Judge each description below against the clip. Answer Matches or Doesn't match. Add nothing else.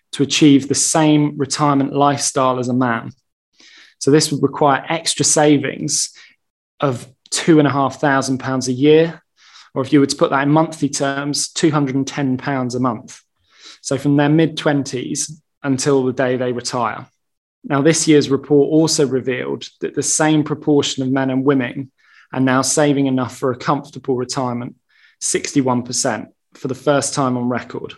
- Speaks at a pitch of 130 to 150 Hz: Matches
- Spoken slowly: Doesn't match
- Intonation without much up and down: Matches